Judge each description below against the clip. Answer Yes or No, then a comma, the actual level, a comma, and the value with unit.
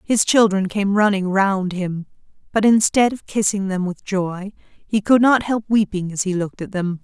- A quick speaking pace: No, average, 195 wpm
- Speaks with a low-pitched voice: No, high, 200 Hz